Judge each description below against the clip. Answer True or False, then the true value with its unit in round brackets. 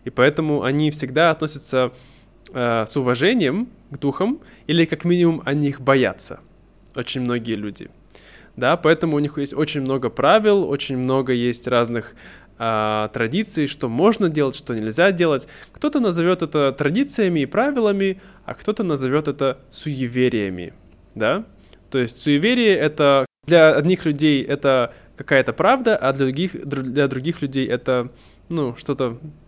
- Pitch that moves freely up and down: False (4.8 semitones)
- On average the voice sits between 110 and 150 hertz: True (140 Hz)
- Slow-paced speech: False (140 wpm)